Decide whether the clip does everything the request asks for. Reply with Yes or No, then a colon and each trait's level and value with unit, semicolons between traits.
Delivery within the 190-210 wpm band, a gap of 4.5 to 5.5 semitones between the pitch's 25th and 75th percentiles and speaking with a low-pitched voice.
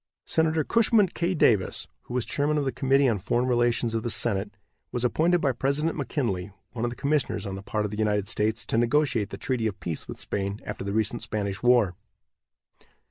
Yes: fast, 205 wpm; average, 5.0 semitones; low, 120 Hz